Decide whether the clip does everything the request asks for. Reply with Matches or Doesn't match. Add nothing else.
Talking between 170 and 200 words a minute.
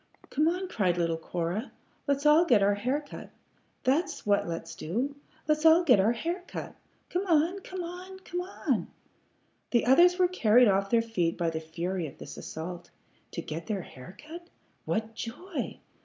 Matches